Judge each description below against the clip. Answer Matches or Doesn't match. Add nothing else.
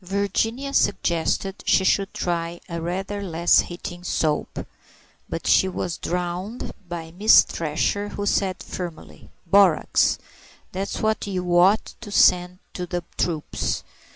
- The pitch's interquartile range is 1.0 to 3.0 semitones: Matches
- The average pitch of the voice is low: Doesn't match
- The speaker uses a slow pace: Matches